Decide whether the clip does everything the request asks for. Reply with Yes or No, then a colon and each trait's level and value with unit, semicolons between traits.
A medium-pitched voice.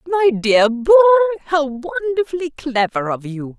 No: very high, 260 Hz